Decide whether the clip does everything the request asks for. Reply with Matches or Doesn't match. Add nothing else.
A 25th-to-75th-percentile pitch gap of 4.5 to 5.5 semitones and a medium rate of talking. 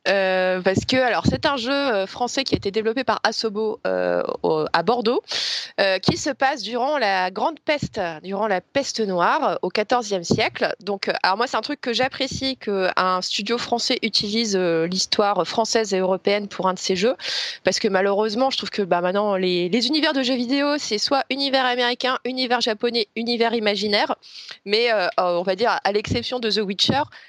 Matches